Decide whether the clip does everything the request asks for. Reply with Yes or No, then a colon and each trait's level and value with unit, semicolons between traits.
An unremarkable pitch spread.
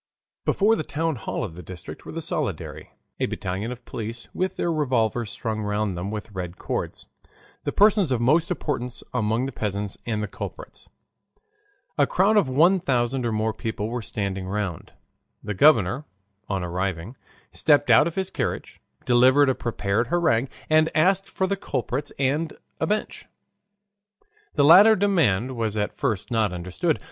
No: wide, 7.0 semitones